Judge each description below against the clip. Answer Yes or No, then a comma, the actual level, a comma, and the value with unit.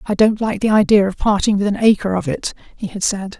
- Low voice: No, high, 205 Hz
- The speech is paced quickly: Yes, fast, 265 wpm